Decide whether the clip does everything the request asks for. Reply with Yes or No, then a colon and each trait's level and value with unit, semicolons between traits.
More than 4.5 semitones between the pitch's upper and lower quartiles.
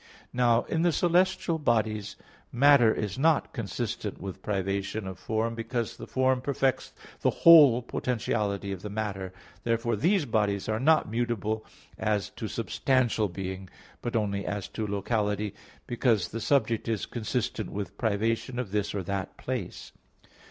No: average, 3.5 semitones